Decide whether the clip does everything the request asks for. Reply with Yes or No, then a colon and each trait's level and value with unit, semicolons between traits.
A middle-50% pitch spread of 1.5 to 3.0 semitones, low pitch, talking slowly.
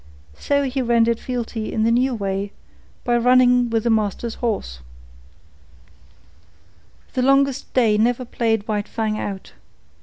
No: narrow, 2.4 semitones; high, 235 Hz; slow, 130 wpm